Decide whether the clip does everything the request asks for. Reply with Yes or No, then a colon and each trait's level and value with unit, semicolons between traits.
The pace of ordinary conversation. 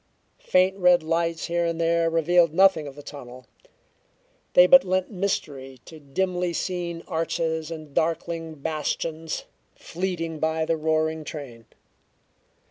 No: slow, 130 wpm